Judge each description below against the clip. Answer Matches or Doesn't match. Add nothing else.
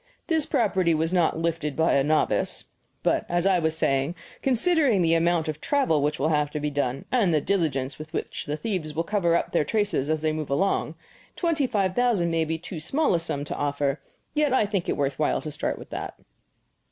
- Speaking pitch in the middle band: Matches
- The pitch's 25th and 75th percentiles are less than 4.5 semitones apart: Doesn't match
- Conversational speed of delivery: Doesn't match